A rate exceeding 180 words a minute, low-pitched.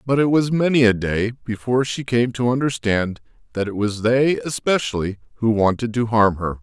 Yes: average, 190 wpm; low, 115 Hz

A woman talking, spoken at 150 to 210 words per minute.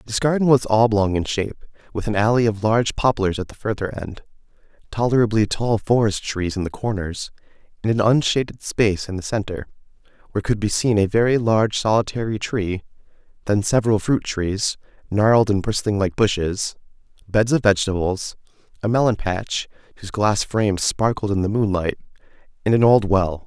No: male; average, 165 wpm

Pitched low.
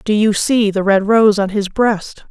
No: high, 205 Hz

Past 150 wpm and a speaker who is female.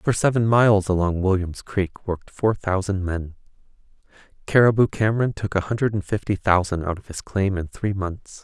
No: average, 180 wpm; male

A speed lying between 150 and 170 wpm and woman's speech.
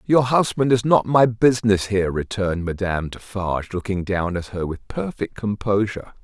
No: average, 165 wpm; male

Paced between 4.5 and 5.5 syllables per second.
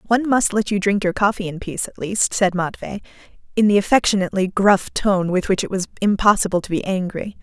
No: 6.0 syllables/s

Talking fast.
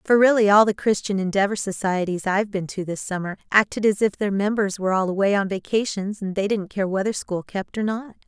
Yes: fast, 225 wpm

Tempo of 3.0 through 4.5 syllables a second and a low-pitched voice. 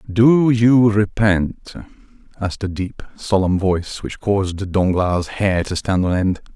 Yes: 4.0 syllables/s; low, 100 Hz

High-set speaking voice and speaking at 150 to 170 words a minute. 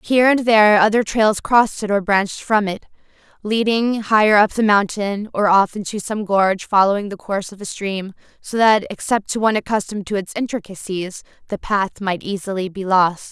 No: high, 205 Hz; average, 190 wpm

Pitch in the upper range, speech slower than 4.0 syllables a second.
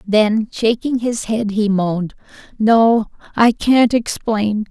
Yes: high, 220 Hz; 3.4 syllables/s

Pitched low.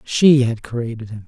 Yes: low, 120 Hz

